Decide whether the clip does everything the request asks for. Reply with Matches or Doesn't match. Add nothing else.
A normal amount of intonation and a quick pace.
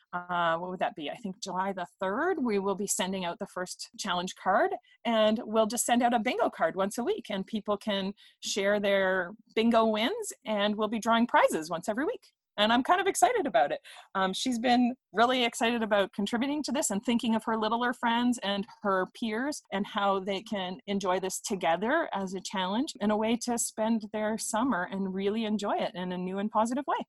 Matches